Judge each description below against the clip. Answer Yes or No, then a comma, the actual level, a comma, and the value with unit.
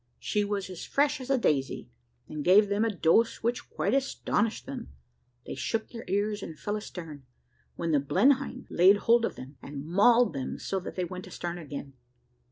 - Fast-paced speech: No, average, 185 wpm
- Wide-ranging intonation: Yes, wide, 6.1 semitones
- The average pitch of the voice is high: Yes, high, 200 Hz